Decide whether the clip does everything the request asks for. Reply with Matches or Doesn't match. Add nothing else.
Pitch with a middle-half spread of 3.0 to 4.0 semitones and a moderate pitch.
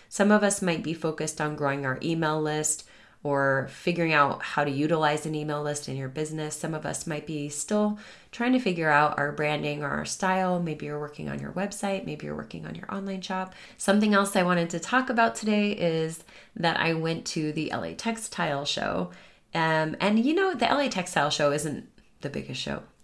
Doesn't match